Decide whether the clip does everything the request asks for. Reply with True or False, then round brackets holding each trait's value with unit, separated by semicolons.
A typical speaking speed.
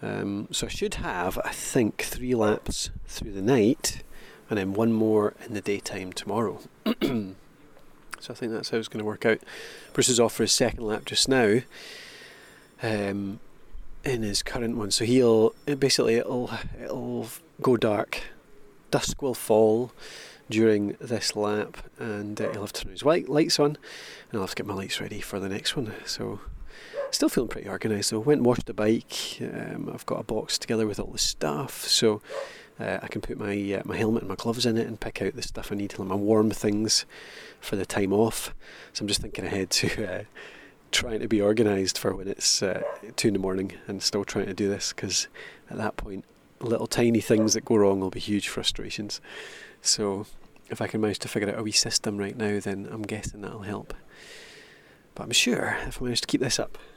False (210 wpm)